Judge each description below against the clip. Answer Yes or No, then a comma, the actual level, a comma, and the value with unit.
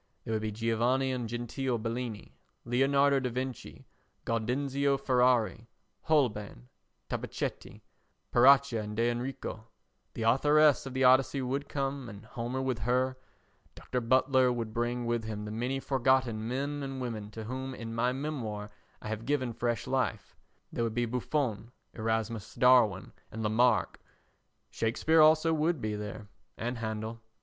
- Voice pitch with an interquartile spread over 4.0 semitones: No, average, 3.0 semitones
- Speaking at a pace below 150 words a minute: Yes, average, 140 wpm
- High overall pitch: No, low, 120 Hz